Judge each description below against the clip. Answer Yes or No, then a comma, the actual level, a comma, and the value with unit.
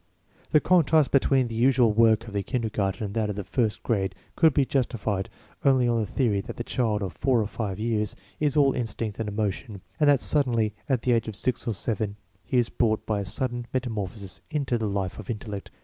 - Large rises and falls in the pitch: No, average, 3.5 semitones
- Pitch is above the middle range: No, low, 115 Hz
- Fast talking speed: Yes, fast, 225 wpm